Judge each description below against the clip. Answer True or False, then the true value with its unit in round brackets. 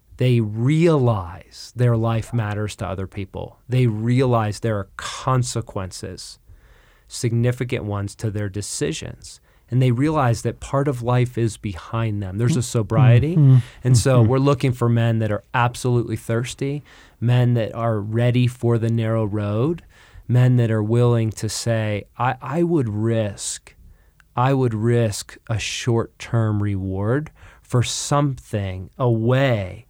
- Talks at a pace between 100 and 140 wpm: True (135 wpm)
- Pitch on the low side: True (115 Hz)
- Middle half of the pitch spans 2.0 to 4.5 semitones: True (2.8 semitones)